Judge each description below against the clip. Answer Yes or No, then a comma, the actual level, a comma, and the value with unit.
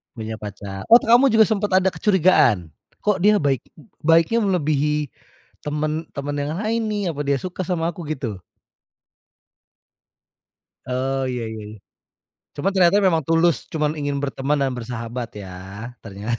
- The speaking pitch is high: No, medium, 150 Hz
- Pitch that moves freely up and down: Yes, wide, 6.8 semitones